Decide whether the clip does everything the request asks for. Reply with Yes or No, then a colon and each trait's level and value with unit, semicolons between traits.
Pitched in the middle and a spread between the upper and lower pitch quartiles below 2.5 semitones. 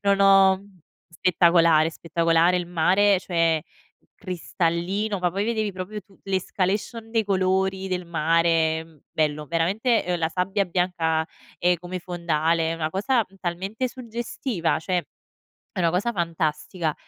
No: medium, 180 Hz; average, 2.8 semitones